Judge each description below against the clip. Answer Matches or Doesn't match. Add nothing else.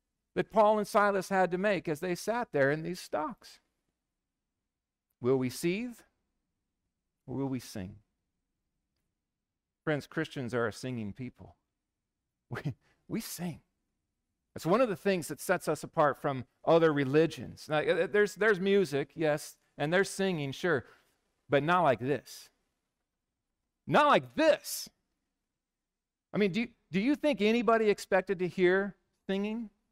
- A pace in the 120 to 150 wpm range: Matches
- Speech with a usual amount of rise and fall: Doesn't match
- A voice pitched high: Doesn't match